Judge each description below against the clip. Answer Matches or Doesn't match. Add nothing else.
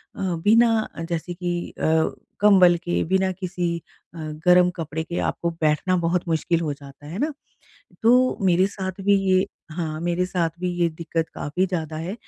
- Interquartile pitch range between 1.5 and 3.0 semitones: Matches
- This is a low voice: Doesn't match